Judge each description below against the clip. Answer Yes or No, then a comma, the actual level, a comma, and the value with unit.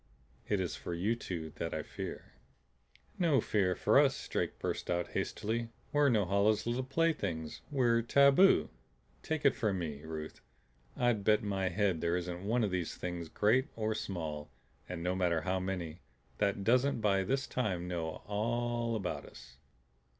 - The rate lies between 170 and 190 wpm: No, average, 160 wpm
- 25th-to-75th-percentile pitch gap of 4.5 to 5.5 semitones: Yes, average, 5.2 semitones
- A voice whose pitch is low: Yes, low, 100 Hz